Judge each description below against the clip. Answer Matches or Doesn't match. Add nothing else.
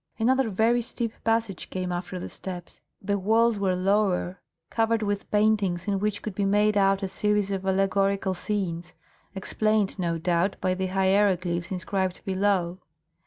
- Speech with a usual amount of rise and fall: Doesn't match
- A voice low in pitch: Doesn't match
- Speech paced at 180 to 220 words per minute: Doesn't match